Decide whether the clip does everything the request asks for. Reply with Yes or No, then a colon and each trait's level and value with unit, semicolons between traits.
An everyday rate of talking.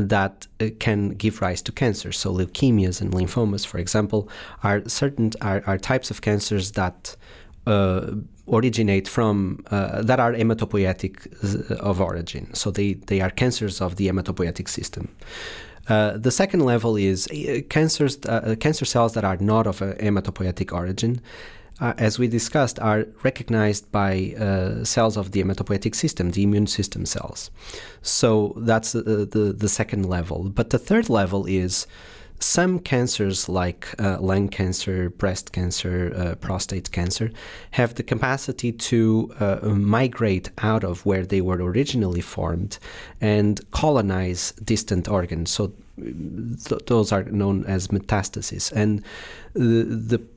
Yes: average, 145 wpm